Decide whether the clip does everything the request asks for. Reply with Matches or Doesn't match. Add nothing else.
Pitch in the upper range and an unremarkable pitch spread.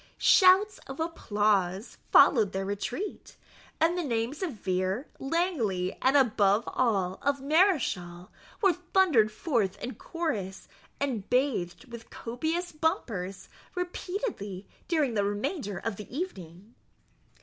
Doesn't match